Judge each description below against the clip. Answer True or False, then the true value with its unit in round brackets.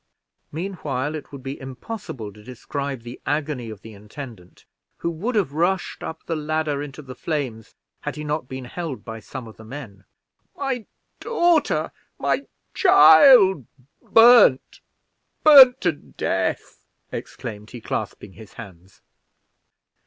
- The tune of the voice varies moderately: False (7.0 semitones)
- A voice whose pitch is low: False (145 Hz)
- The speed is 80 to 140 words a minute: True (135 wpm)